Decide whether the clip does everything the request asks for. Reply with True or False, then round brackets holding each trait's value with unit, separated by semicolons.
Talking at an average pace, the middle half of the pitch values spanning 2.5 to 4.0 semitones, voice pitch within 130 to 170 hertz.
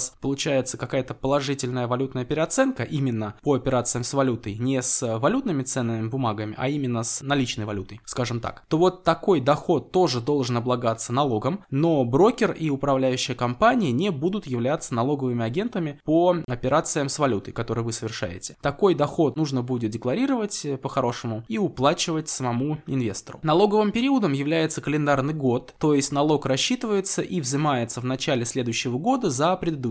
False (150 wpm; 4.4 semitones; 135 Hz)